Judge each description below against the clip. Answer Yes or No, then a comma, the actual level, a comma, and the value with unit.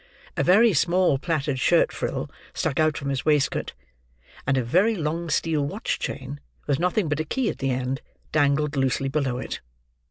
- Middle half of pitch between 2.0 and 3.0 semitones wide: No, average, 3.8 semitones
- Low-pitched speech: No, medium, 150 Hz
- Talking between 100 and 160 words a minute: No, average, 180 wpm